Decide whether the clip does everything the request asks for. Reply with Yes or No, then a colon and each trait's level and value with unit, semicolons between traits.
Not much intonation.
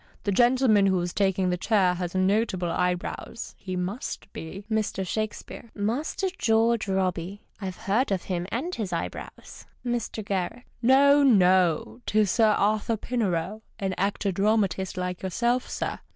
No: average, 3.6 semitones